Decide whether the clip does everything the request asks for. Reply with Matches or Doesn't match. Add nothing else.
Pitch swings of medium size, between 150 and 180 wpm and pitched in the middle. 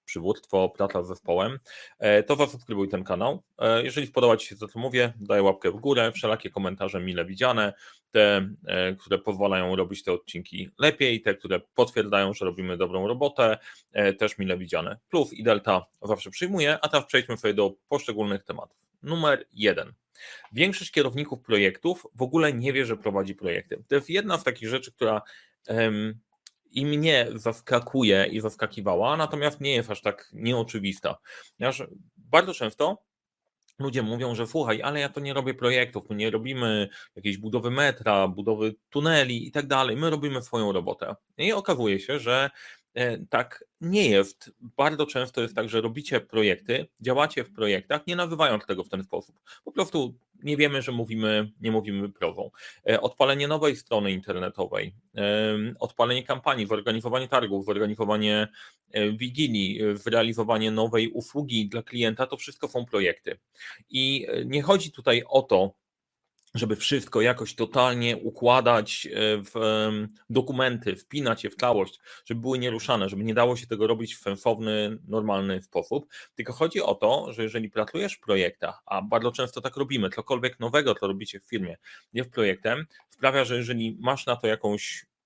Doesn't match